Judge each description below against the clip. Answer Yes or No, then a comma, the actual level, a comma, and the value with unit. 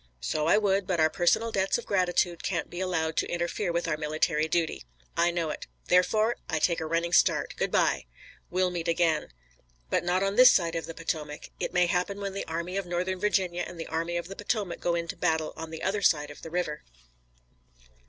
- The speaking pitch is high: No, medium, 175 Hz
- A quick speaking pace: Yes, fast, 215 wpm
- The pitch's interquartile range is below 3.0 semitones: Yes, narrow, 2.5 semitones